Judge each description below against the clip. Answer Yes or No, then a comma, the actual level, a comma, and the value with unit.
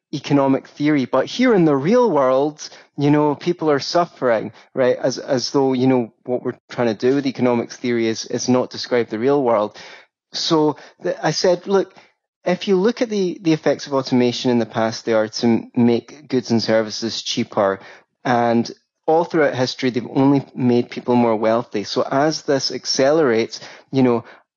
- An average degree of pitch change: Yes, average, 4.1 semitones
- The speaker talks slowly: No, average, 185 wpm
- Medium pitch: No, low, 130 Hz